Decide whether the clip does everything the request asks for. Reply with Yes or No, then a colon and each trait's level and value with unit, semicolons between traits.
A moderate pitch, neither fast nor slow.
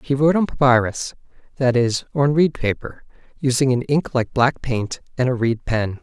No: low, 130 Hz; average, 180 wpm